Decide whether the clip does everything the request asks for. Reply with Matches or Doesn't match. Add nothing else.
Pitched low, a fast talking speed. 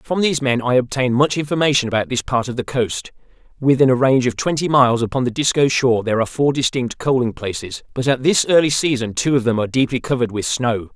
Matches